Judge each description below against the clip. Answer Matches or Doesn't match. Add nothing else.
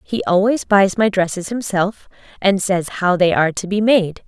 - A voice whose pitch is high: Matches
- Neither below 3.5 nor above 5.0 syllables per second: Matches